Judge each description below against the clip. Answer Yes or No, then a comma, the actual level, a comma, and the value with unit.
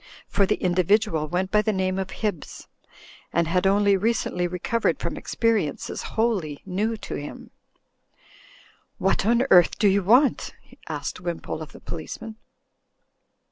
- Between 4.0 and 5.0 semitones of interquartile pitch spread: No, average, 3.4 semitones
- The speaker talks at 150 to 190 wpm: No, average, 140 wpm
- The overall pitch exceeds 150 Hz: Yes, high, 190 Hz